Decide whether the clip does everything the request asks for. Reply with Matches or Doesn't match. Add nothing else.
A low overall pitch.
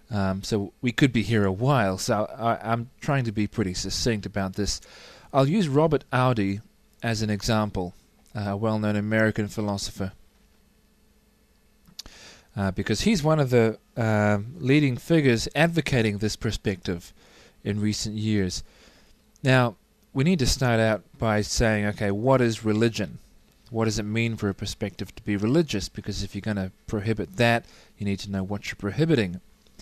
Matches